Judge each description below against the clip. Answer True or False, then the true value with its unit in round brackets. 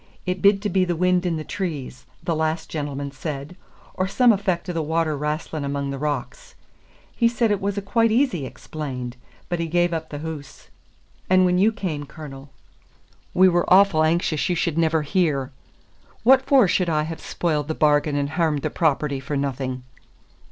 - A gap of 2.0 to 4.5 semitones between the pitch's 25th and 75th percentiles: True (4.2 semitones)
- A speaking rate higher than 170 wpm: True (190 wpm)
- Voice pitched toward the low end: False (160 Hz)